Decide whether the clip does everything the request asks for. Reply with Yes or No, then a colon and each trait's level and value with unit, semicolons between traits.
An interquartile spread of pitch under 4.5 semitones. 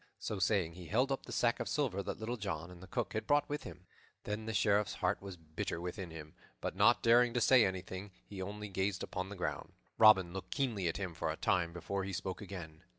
Yes: average, 3.5 semitones